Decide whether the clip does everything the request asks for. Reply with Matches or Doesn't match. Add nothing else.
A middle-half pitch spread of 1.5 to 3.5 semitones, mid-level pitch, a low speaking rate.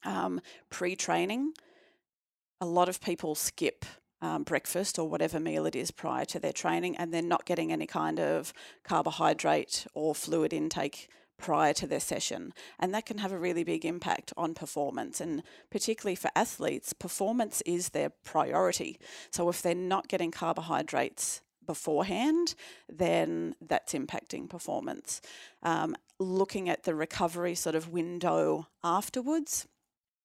Doesn't match